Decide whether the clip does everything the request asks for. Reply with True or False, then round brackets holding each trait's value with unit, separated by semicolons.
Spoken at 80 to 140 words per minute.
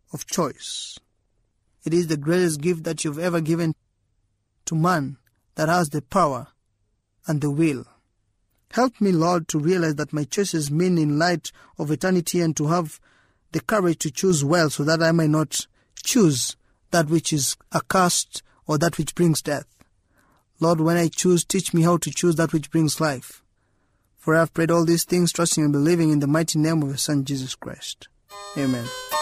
False (185 wpm)